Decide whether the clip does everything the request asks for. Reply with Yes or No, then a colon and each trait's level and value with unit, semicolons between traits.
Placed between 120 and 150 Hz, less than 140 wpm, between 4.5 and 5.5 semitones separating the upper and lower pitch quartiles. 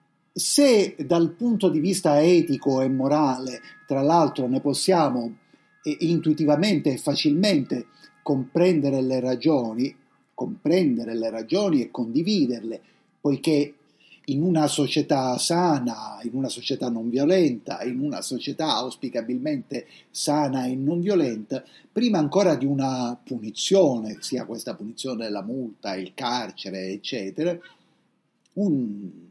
Yes: medium, 140 Hz; slow, 115 wpm; average, 5.0 semitones